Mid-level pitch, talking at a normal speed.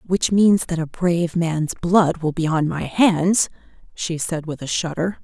Yes: medium, 170 Hz; average, 195 wpm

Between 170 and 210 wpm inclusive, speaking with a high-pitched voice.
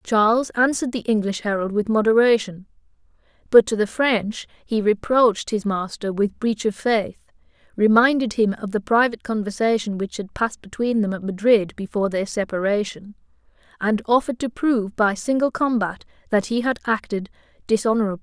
No: average, 155 wpm; high, 220 Hz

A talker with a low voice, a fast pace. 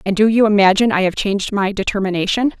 No: high, 205 Hz; fast, 210 wpm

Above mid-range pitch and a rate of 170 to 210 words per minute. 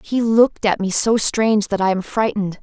No: high, 210 Hz; fast, 230 wpm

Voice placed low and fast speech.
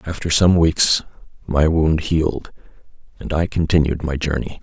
No: very low, 80 Hz; average, 145 wpm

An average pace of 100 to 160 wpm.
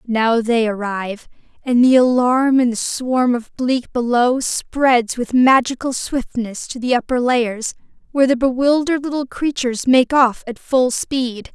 Yes: average, 155 wpm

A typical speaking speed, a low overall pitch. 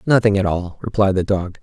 No: fast, 220 wpm; low, 100 Hz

